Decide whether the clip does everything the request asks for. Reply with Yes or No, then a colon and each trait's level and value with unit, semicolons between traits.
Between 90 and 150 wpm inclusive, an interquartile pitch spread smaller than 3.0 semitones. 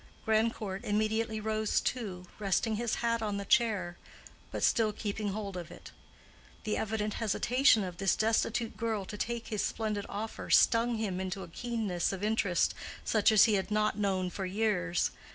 No: average, 170 wpm; narrow, 2.4 semitones